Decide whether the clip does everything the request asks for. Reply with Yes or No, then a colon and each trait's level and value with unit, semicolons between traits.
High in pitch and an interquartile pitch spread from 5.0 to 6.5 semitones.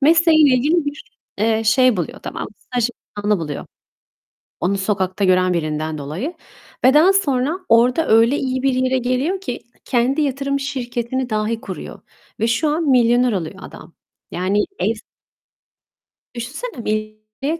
No: high, 245 Hz; average, 4.5 semitones